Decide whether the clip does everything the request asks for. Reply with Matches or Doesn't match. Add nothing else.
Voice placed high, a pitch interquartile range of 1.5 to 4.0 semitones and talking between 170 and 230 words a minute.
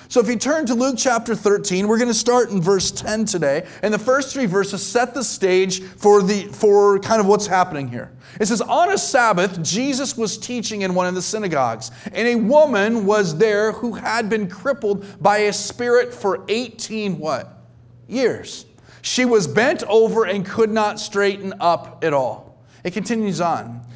Matches